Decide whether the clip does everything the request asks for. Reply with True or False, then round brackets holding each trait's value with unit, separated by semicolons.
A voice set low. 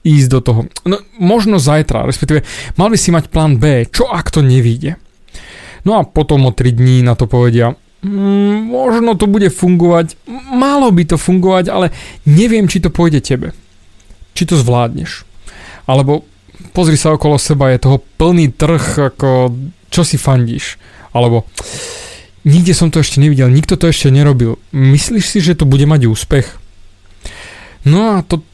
False (150 Hz)